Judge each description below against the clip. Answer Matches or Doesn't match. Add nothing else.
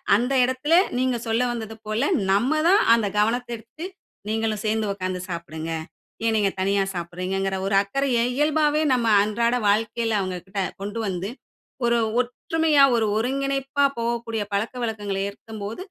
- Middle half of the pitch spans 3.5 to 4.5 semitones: Matches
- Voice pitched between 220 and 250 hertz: Matches